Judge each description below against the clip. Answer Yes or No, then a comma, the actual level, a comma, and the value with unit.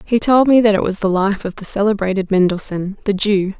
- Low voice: No, high, 200 Hz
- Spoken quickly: Yes, fast, 235 wpm